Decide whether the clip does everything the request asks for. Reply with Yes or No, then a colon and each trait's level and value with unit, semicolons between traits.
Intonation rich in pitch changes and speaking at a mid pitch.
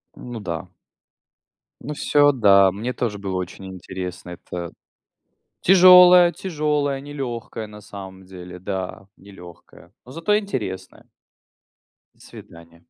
No: wide, 7.7 semitones; low, 100 Hz